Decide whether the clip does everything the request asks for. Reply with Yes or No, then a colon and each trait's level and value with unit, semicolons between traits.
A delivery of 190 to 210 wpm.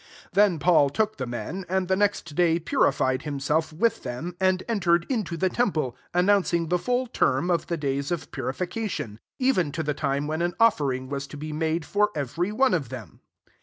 Yes: average, 200 wpm